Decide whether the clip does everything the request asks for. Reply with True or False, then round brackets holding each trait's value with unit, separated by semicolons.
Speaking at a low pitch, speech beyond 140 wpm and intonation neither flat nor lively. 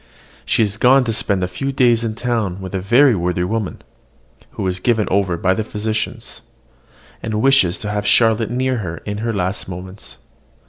True (105 Hz; 190 wpm; 3.8 semitones)